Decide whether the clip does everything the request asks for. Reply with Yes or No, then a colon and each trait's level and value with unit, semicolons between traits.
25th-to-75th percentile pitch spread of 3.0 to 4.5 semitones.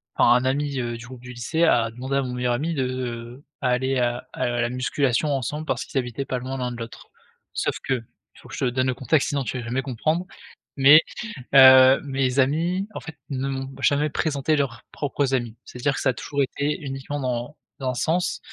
No: narrow, 2.4 semitones